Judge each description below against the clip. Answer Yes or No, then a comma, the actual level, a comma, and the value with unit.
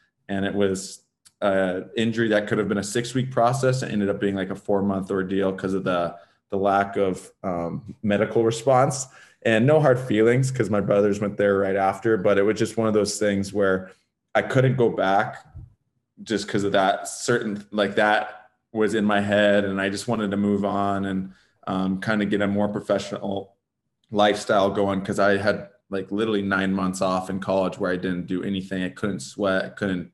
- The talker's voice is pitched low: Yes, low, 100 Hz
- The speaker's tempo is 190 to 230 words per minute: Yes, average, 200 wpm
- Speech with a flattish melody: Yes, narrow, 1.8 semitones